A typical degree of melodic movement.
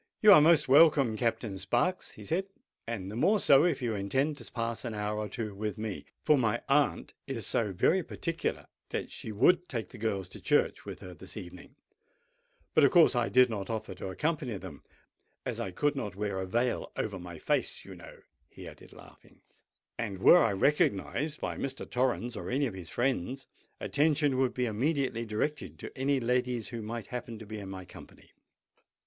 Yes: average, 5.0 semitones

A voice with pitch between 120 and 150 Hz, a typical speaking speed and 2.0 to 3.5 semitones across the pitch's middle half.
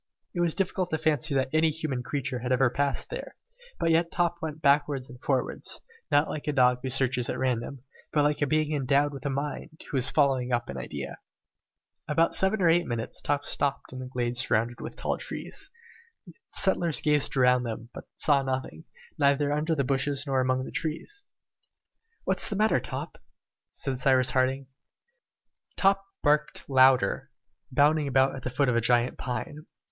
Yes: medium, 140 Hz; average, 185 wpm; average, 3.2 semitones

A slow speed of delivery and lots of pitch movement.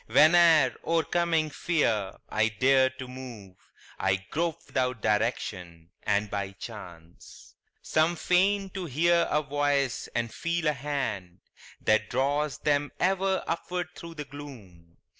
Yes: slow, 125 wpm; wide, 7.4 semitones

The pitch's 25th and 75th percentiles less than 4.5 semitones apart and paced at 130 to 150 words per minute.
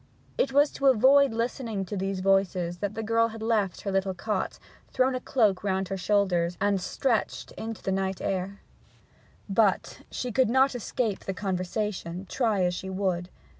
No: average, 3.3 semitones; average, 180 wpm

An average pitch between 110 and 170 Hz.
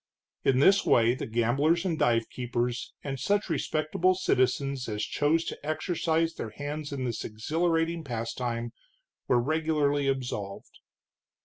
Yes: medium, 140 Hz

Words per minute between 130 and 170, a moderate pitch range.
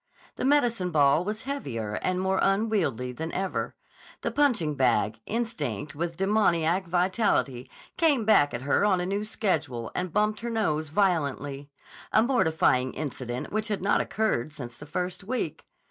No: average, 160 wpm; wide, 7.1 semitones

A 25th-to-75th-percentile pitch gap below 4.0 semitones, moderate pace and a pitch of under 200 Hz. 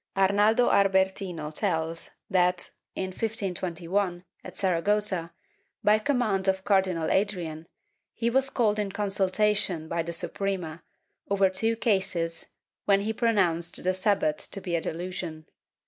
No: average, 3.4 semitones; slow, 125 wpm; high, 190 Hz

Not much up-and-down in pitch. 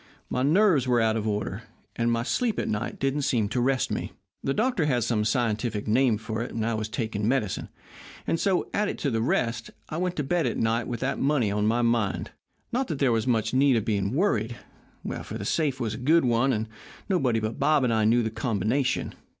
No: average, 3.6 semitones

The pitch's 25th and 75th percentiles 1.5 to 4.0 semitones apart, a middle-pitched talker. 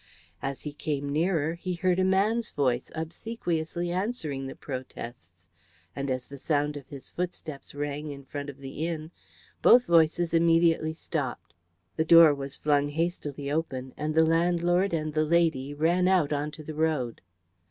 Yes: average, 3.1 semitones; medium, 155 Hz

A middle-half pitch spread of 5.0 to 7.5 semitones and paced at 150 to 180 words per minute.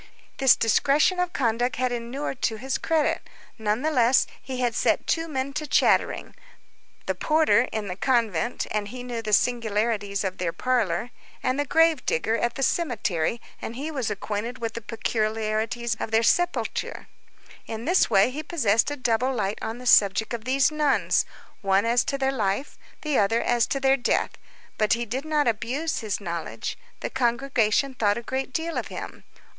No: average, 3.8 semitones; average, 175 wpm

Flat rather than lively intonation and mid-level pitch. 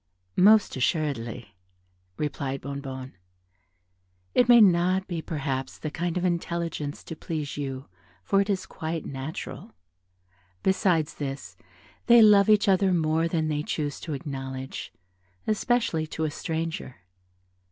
No: average, 4.8 semitones; medium, 160 Hz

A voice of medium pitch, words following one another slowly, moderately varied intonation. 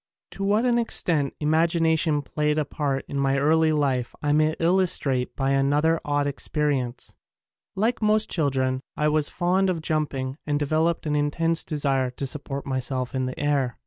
No: medium, 150 Hz; average, 170 wpm; average, 3.0 semitones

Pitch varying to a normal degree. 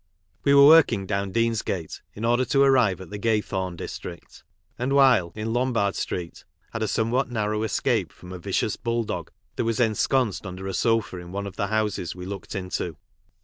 Yes: average, 3.7 semitones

